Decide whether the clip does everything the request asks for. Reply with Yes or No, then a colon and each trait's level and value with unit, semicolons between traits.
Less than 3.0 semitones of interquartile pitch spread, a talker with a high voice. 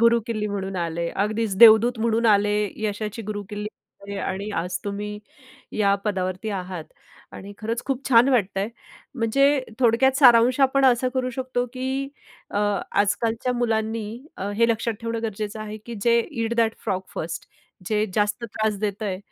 Yes: narrow, 2.5 semitones; high, 220 Hz